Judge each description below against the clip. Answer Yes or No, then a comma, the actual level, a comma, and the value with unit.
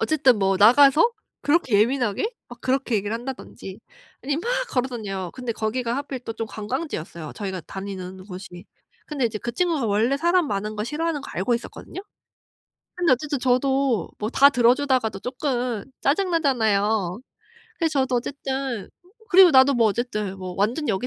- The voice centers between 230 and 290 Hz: Yes, high, 245 Hz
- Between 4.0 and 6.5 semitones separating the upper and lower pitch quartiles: Yes, average, 5.1 semitones